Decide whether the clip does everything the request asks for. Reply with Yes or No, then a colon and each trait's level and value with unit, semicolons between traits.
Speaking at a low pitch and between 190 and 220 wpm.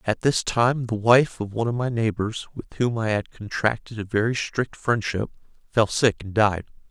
Yes: low, 115 Hz; average, 200 wpm